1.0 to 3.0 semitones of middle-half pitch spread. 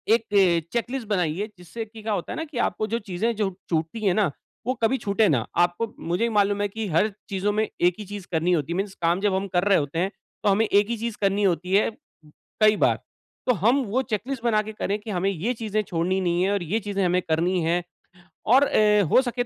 No: average, 3.6 semitones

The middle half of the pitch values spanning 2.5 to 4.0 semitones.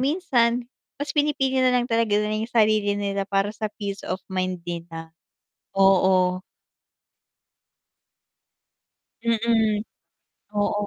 Yes: average, 3.2 semitones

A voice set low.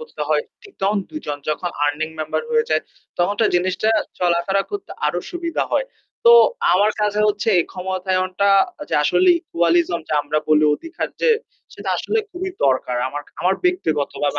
No: medium, 185 Hz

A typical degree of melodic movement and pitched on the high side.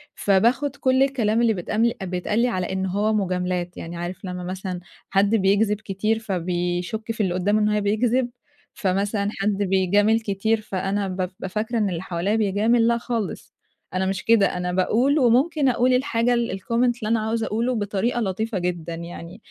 Yes: average, 3.5 semitones; high, 205 Hz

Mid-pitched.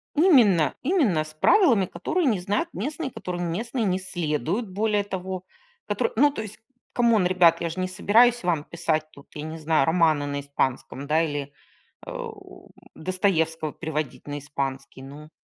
Yes: medium, 175 Hz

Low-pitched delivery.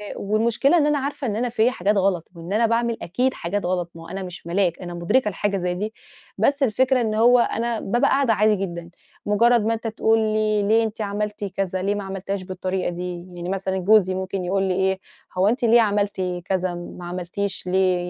No: high, 200 Hz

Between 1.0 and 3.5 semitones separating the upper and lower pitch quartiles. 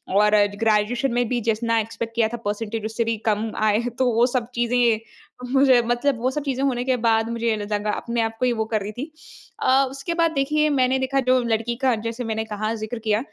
Yes: narrow, 2.5 semitones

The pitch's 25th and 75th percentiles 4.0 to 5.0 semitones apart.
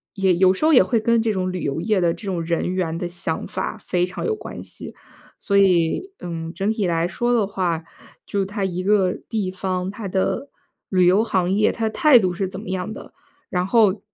No: average, 3.1 semitones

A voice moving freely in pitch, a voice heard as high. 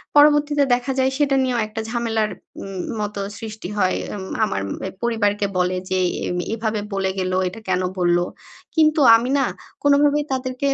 Yes: wide, 5.9 semitones; high, 220 Hz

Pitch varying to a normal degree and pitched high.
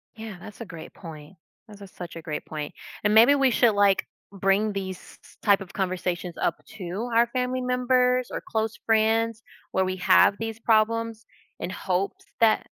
Yes: average, 3.5 semitones; high, 215 Hz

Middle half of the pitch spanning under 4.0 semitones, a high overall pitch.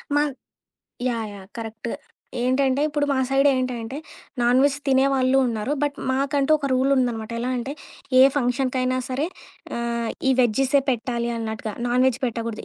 Yes: narrow, 2.5 semitones; very high, 255 Hz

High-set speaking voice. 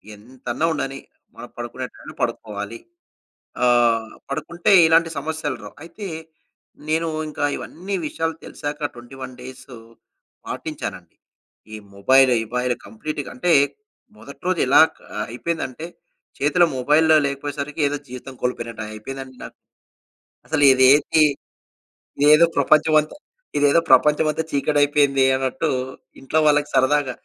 No: medium, 145 Hz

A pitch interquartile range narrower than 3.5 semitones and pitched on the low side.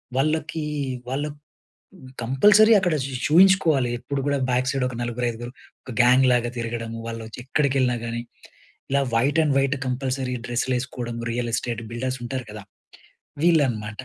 Yes: average, 2.9 semitones; low, 130 Hz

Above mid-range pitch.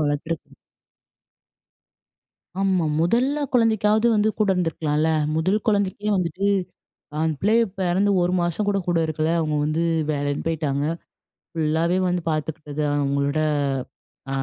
No: medium, 170 Hz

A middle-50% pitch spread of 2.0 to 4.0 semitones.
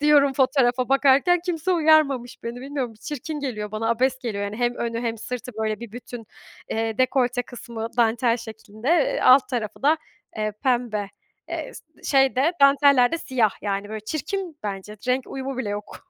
Yes: average, 3.6 semitones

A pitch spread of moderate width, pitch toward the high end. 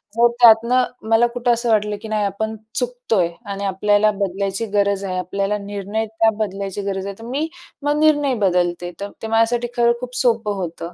Yes: average, 3.2 semitones; high, 215 Hz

